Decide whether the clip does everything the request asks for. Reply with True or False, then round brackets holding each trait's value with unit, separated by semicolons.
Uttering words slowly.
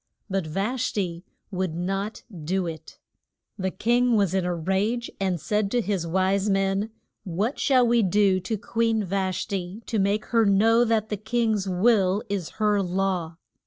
False (170 wpm)